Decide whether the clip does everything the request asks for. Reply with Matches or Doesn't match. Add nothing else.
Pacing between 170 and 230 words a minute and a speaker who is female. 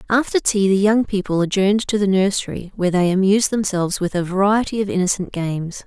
Matches